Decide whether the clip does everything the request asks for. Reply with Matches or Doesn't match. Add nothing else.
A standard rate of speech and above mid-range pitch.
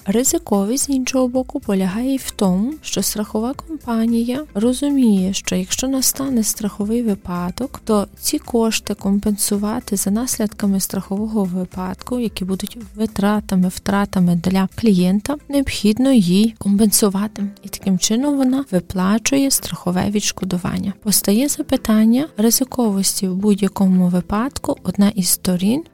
Matches